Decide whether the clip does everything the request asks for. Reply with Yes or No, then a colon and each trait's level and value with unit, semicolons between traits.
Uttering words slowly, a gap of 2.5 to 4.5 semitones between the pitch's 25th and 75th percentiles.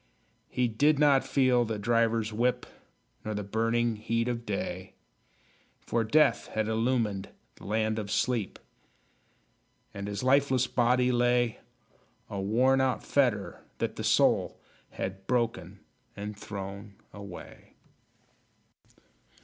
Yes: slow, 115 wpm; average, 3.3 semitones